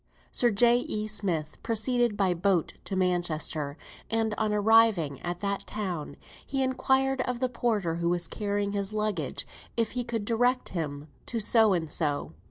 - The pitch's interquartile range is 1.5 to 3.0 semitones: No, average, 4.9 semitones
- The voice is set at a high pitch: Yes, high, 205 Hz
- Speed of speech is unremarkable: Yes, average, 165 wpm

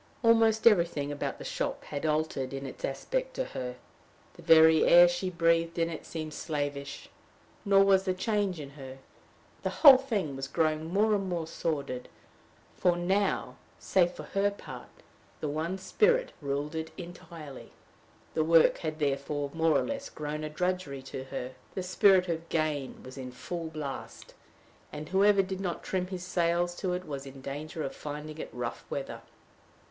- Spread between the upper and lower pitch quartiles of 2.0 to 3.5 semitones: No, average, 4.3 semitones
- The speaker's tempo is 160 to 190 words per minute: Yes, average, 170 wpm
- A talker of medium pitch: Yes, medium, 165 Hz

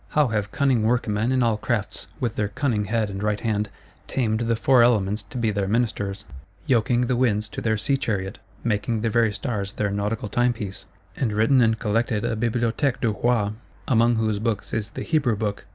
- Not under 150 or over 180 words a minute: No, average, 190 wpm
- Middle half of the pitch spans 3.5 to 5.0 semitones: No, narrow, 2.5 semitones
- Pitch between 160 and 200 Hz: No, low, 110 Hz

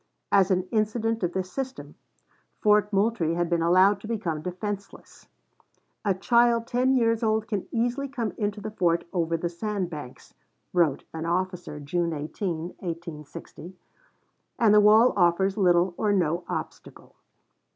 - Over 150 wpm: No, average, 145 wpm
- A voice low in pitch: No, high, 190 Hz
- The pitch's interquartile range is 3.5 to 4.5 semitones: Yes, average, 4.0 semitones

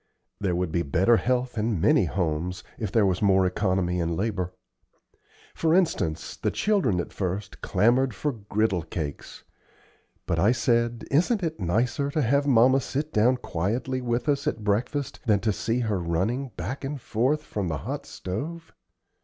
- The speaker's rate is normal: Yes, average, 165 wpm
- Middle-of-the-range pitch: No, low, 110 Hz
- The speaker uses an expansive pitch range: Yes, wide, 6.0 semitones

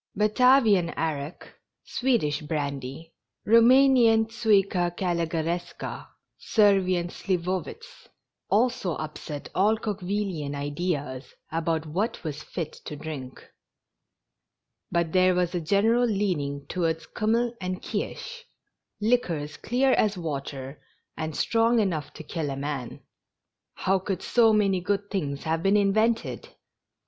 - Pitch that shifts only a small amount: No, wide, 5.5 semitones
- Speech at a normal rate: No, slow, 115 wpm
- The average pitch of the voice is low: No, medium, 180 Hz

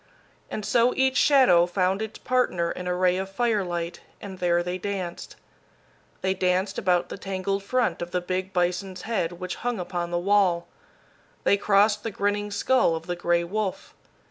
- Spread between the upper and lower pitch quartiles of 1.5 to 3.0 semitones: Yes, narrow, 2.6 semitones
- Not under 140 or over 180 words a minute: Yes, average, 170 wpm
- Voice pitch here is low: No, medium, 185 Hz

